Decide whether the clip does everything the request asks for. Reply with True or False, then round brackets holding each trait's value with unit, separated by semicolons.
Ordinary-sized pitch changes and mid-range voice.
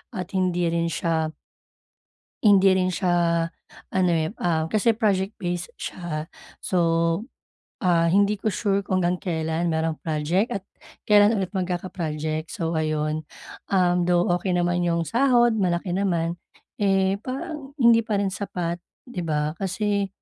True (3.0 semitones; 180 Hz)